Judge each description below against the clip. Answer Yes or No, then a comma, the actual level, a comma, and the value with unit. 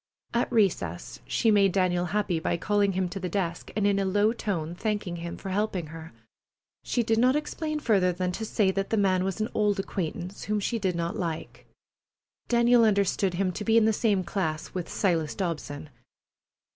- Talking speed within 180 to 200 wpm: Yes, average, 195 wpm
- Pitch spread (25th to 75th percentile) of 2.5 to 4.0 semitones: Yes, average, 3.5 semitones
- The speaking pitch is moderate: No, high, 195 Hz